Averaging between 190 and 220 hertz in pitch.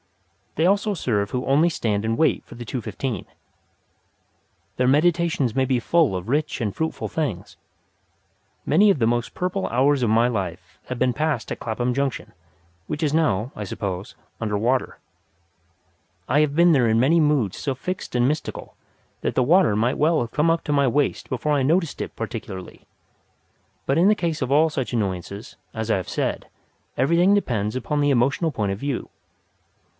No: low, 130 Hz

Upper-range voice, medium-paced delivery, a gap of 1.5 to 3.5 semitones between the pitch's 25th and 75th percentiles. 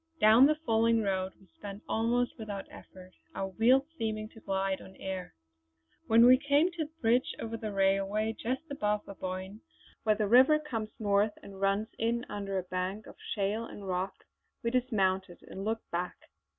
Yes: high, 215 Hz; average, 175 wpm; average, 3.0 semitones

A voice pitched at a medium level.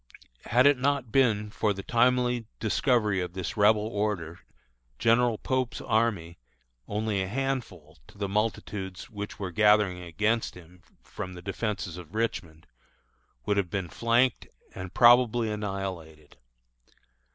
No: low, 105 Hz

